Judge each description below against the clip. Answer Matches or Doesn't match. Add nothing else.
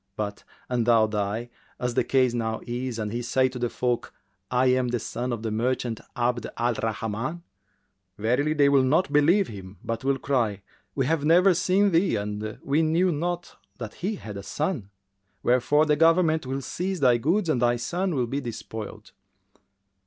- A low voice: Matches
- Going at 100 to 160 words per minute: Doesn't match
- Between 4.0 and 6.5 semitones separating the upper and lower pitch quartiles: Matches